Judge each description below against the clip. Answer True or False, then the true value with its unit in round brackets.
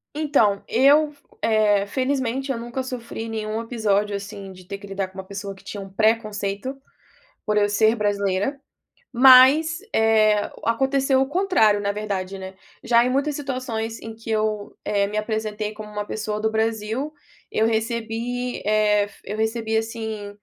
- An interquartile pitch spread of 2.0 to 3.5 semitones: True (3.2 semitones)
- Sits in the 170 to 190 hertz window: False (220 Hz)